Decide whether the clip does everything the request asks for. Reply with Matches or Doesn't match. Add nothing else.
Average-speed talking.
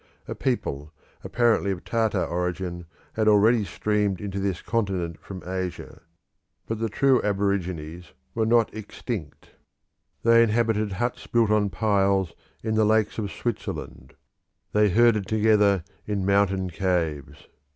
Doesn't match